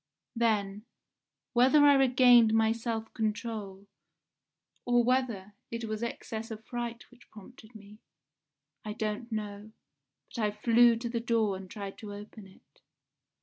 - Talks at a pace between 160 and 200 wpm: No, average, 140 wpm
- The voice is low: No, high, 225 Hz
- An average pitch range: No, narrow, 2.2 semitones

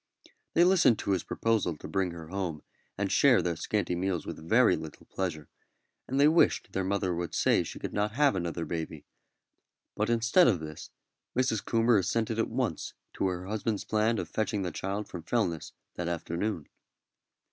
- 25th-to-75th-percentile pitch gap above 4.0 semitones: Yes, average, 4.7 semitones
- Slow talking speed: No, average, 180 wpm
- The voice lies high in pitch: No, very low, 95 Hz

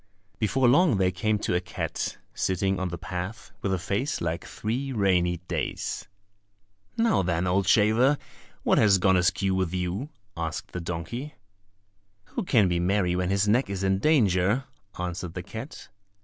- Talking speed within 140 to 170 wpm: Yes, average, 165 wpm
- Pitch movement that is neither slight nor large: Yes, average, 3.7 semitones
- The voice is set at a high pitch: No, very low, 95 Hz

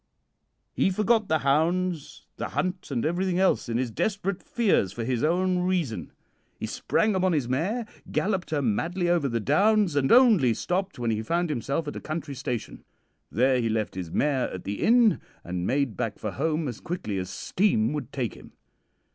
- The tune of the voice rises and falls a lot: Yes, wide, 7.3 semitones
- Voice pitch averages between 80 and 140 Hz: No, medium, 155 Hz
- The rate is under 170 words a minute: No, average, 185 wpm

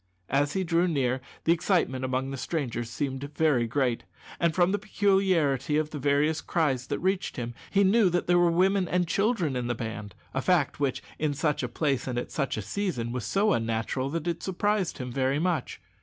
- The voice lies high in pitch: No, medium, 150 Hz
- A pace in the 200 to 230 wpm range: Yes, fast, 205 wpm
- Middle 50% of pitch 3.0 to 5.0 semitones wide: No, wide, 5.4 semitones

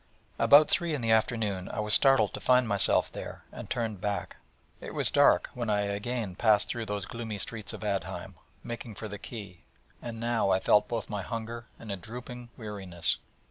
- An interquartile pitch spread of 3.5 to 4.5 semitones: No, narrow, 2.5 semitones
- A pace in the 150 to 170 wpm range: No, average, 190 wpm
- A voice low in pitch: Yes, low, 110 Hz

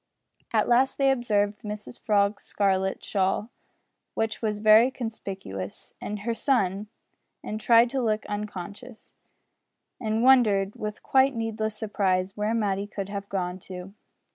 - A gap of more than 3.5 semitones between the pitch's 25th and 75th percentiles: No, narrow, 2.6 semitones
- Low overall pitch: No, high, 210 Hz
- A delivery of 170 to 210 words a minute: No, slow, 135 wpm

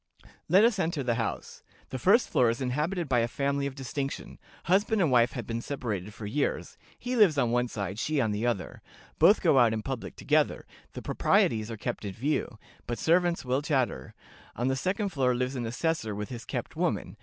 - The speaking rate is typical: No, fast, 210 wpm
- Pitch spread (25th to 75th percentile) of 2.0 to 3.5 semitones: No, average, 4.9 semitones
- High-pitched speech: No, low, 130 Hz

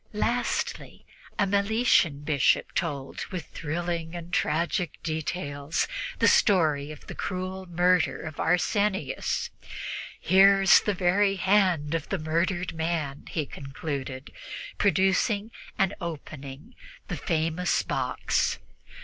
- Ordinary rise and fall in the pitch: Yes, average, 3.9 semitones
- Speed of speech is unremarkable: No, slow, 110 wpm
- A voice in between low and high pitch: Yes, medium, 175 Hz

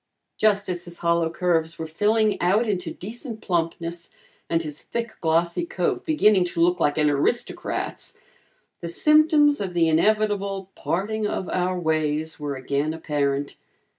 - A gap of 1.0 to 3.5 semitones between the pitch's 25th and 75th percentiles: No, average, 4.5 semitones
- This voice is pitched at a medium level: Yes, medium, 175 Hz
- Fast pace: No, average, 145 wpm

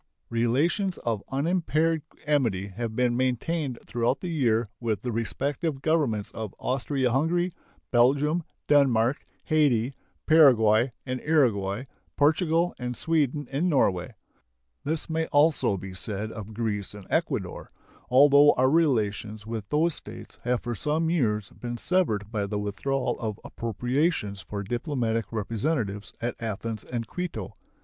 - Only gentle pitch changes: No, wide, 5.4 semitones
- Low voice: Yes, low, 125 Hz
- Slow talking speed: Yes, slow, 130 wpm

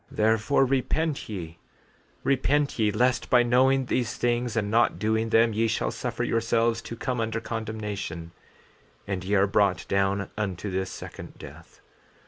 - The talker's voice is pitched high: No, low, 110 Hz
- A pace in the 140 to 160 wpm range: Yes, average, 155 wpm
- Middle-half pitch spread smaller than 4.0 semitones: Yes, average, 3.2 semitones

